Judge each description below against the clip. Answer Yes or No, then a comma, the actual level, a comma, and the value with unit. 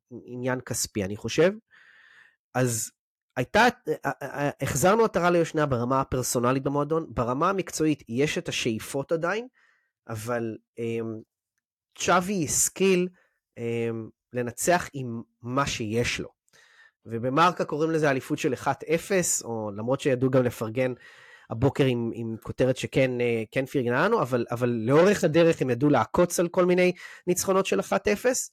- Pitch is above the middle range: No, low, 135 Hz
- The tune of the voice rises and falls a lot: Yes, wide, 6.1 semitones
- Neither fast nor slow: Yes, average, 125 wpm